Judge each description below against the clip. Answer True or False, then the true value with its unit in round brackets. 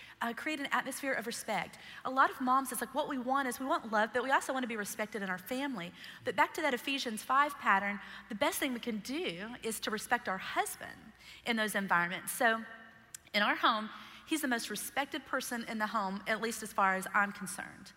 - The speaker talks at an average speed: False (230 wpm)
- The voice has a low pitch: False (235 Hz)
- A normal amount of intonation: True (4.1 semitones)